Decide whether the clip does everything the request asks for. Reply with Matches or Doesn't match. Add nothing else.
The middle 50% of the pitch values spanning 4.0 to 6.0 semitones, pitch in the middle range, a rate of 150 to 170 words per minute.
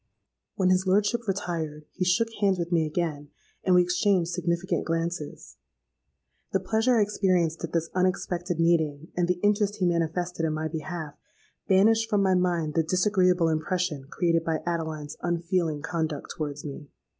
Doesn't match